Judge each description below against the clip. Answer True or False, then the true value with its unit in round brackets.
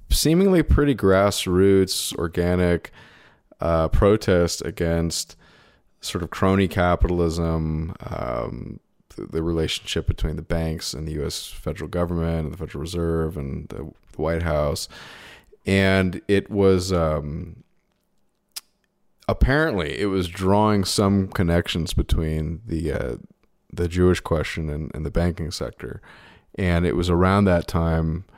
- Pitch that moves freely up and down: False (2.9 semitones)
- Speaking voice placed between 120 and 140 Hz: False (85 Hz)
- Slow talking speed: True (125 wpm)